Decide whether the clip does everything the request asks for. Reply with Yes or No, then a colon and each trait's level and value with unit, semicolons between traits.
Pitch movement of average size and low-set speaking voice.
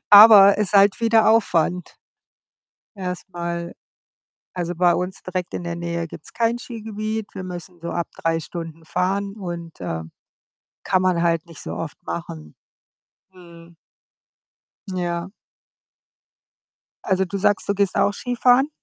No: average, 3.0 semitones; medium, 180 Hz